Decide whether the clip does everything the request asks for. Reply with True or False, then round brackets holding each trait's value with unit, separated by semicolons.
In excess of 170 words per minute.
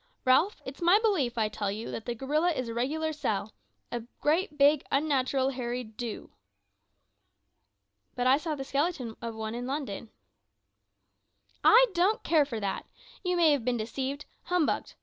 False (160 wpm)